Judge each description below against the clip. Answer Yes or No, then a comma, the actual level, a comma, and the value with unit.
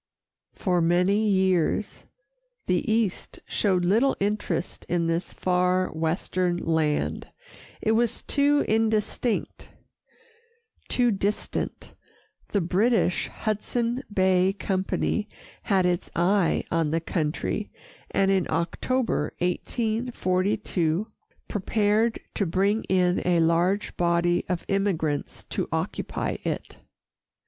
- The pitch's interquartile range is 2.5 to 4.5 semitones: Yes, average, 3.4 semitones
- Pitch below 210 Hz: Yes, high, 190 Hz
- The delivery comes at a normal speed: No, slow, 100 wpm